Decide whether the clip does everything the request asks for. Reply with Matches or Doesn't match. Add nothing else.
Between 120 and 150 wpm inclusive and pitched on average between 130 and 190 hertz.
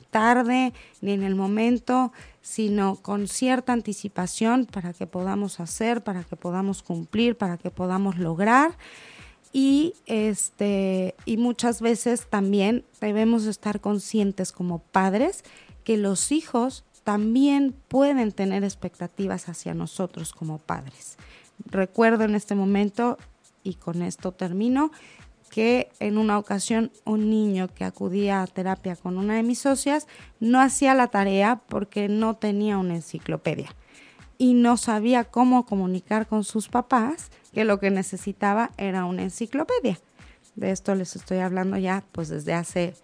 Doesn't match